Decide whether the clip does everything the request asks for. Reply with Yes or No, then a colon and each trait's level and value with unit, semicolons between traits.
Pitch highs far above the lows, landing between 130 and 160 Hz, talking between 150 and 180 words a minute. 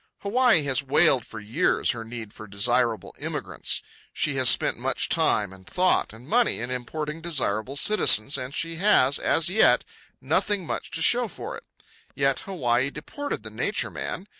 Yes: wide, 6.5 semitones; medium, 140 Hz; average, 165 wpm